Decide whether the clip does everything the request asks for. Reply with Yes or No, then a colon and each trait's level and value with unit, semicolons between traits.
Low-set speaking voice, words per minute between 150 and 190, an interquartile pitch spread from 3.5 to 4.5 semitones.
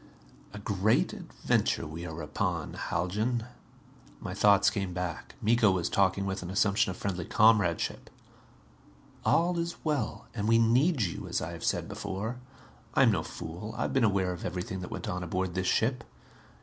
Yes: low, 100 Hz; average, 175 wpm; average, 3.8 semitones